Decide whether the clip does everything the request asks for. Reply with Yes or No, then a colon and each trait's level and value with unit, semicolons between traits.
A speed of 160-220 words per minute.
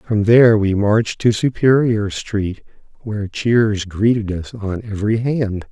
No: average, 145 wpm